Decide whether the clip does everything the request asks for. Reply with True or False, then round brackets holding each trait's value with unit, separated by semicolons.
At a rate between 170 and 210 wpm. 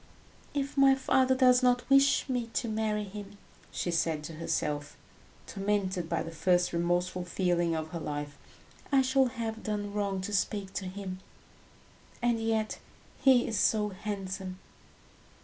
False (150 wpm)